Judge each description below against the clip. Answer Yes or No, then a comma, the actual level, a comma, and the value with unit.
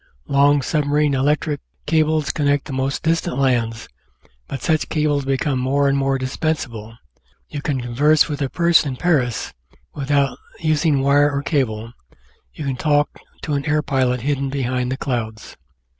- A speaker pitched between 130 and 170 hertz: Yes, medium, 140 Hz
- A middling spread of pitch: No, narrow, 2.3 semitones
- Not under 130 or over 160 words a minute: Yes, average, 155 wpm